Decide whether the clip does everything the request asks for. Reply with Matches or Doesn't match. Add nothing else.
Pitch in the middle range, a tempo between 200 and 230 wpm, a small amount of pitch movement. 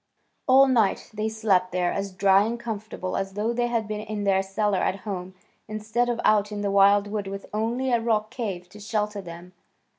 Doesn't match